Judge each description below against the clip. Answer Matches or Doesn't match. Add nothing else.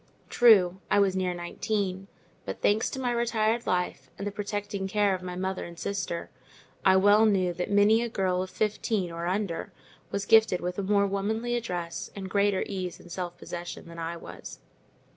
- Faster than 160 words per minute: Matches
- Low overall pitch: Doesn't match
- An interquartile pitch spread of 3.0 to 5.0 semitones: Doesn't match